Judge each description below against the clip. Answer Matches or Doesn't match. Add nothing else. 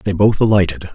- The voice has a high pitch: Doesn't match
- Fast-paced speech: Doesn't match